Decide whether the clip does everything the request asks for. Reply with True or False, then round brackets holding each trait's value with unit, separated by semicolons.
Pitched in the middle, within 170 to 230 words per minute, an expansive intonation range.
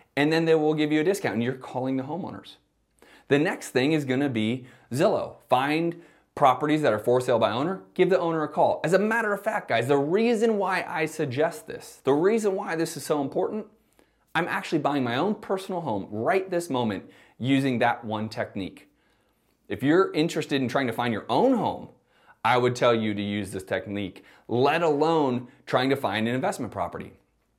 True (150 Hz; 200 wpm; 5.7 semitones)